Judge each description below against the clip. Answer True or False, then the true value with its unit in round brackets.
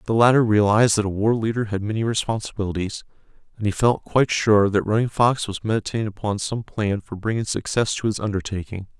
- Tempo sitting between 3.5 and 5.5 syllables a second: False (6.1 syllables/s)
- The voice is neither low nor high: False (110 Hz)